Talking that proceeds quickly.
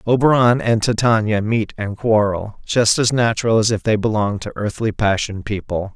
No: average, 170 wpm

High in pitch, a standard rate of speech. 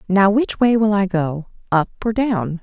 Yes: high, 200 Hz; average, 185 wpm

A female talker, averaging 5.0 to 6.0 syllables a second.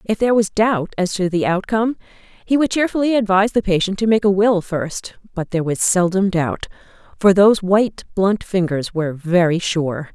Yes: female; 5.4 syllables/s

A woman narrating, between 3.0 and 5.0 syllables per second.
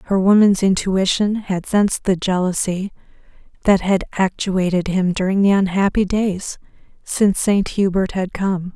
Yes: female; 4.5 syllables/s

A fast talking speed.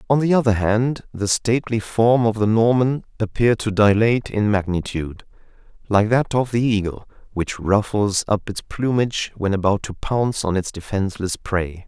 No: average, 165 wpm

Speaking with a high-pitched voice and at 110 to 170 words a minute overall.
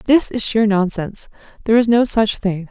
No: high, 215 Hz; average, 200 wpm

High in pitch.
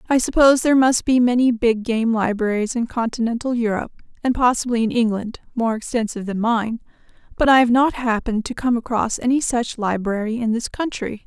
Yes: high, 235 Hz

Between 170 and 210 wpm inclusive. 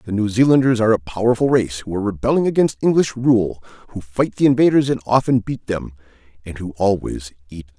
Yes: average, 200 wpm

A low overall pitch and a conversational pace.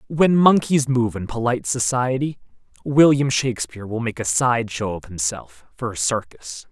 Yes: low, 115 Hz; average, 160 wpm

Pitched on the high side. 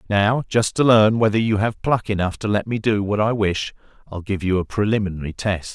No: low, 105 Hz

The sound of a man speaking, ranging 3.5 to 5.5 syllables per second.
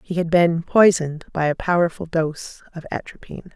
No: female; 5.3 syllables/s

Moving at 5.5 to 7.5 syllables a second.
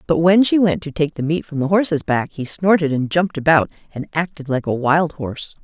Yes: 5.6 syllables/s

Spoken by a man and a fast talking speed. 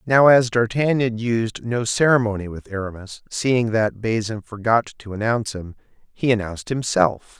No: male; average, 145 wpm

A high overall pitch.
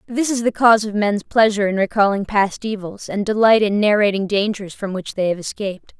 Yes: high, 205 Hz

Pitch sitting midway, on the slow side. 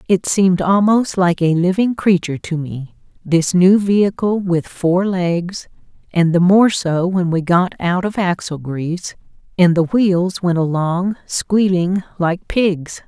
No: medium, 180 Hz; average, 155 wpm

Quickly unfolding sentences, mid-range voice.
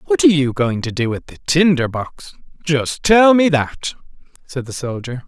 No: average, 195 wpm; medium, 150 Hz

